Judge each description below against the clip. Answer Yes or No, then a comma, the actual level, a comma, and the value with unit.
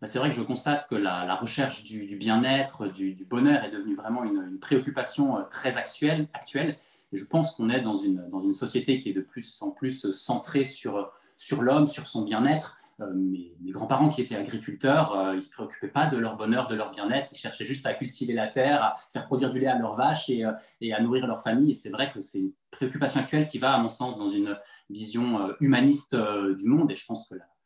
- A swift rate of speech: Yes, fast, 245 wpm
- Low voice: Yes, low, 130 Hz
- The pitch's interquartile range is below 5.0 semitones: No, average, 5.3 semitones